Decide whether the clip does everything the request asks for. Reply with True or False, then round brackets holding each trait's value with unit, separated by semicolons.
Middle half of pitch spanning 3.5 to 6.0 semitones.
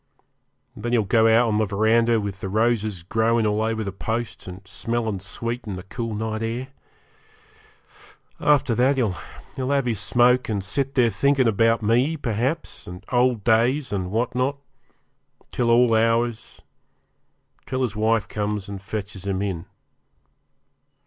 False (2.8 semitones)